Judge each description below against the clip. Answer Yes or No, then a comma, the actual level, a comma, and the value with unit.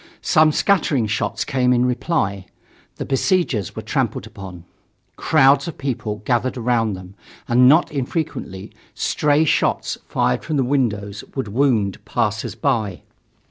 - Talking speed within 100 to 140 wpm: Yes, slow, 135 wpm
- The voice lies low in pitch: Yes, low, 125 Hz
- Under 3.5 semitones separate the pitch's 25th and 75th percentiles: No, average, 5.3 semitones